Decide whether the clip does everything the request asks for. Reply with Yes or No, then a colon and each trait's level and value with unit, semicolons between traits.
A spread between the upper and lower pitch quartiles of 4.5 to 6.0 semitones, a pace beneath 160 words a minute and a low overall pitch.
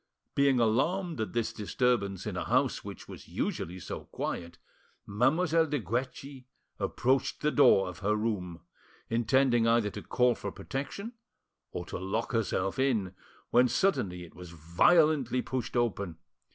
Yes: wide, 5.5 semitones; average, 145 wpm; low, 120 Hz